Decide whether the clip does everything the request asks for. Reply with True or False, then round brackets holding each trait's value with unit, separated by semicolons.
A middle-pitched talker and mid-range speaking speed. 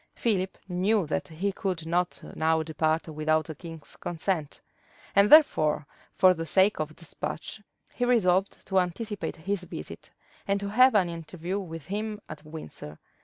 True (180 Hz; 155 wpm)